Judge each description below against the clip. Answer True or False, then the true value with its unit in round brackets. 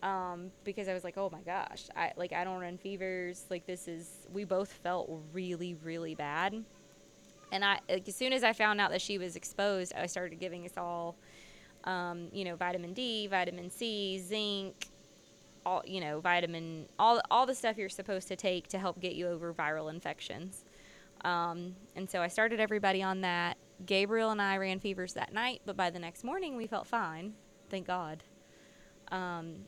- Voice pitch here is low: False (185 Hz)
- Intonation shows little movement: True (2.2 semitones)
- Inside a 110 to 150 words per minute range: False (190 wpm)